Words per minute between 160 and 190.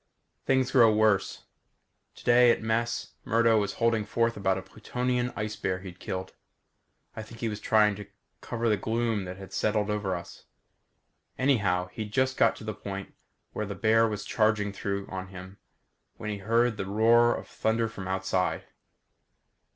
Yes: average, 165 wpm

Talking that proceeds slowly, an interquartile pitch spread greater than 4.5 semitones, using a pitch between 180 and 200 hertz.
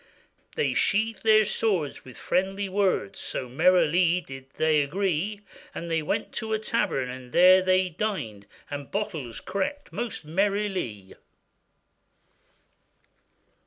Yes: slow, 115 wpm; wide, 5.6 semitones; medium, 185 Hz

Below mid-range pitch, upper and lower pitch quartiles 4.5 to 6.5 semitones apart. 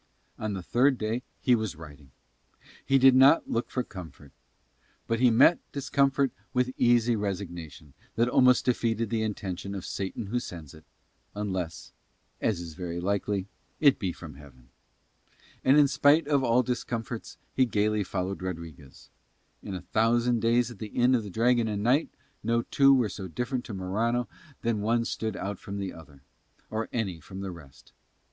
Yes: low, 110 Hz; average, 4.8 semitones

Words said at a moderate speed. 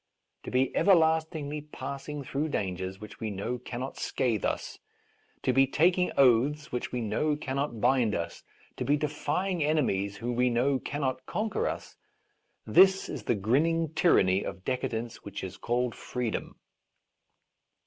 Yes: average, 155 wpm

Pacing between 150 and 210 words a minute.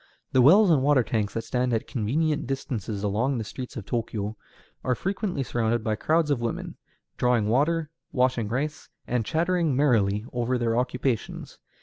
Yes: average, 160 wpm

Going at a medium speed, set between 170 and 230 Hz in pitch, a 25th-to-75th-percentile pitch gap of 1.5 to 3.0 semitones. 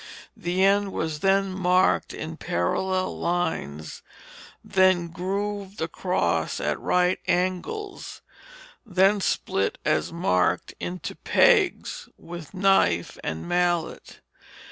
No: slow, 100 wpm; medium, 185 Hz; narrow, 2.5 semitones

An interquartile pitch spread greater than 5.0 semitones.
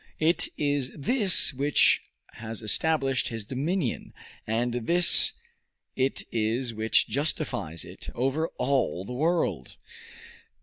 Yes: wide, 5.4 semitones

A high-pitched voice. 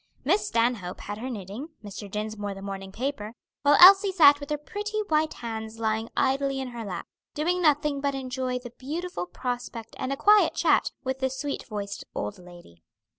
Yes: very high, 255 Hz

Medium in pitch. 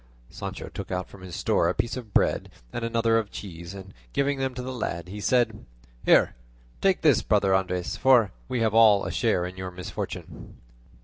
No: low, 105 Hz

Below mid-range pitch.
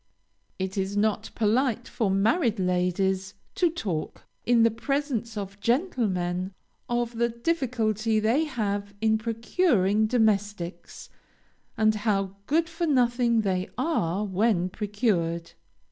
No: high, 215 Hz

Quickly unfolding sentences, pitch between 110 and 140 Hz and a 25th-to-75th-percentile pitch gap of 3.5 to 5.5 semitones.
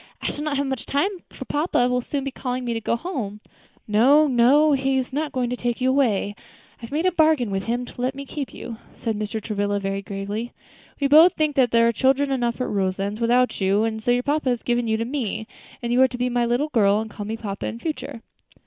No: fast, 250 wpm; high, 245 Hz; average, 3.9 semitones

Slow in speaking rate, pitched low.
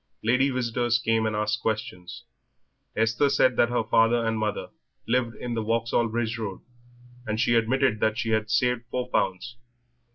No: average, 165 wpm; low, 115 Hz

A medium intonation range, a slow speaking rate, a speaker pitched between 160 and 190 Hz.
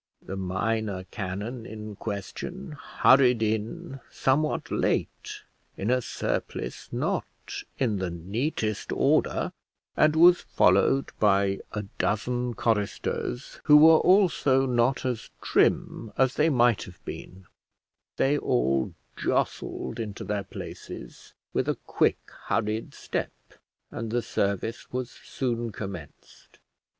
No: average, 4.8 semitones; slow, 115 wpm; low, 115 Hz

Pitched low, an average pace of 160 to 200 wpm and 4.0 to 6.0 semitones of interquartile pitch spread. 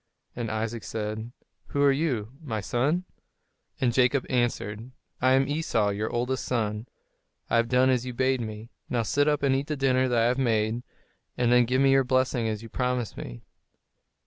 No: low, 125 Hz; average, 190 wpm; average, 2.8 semitones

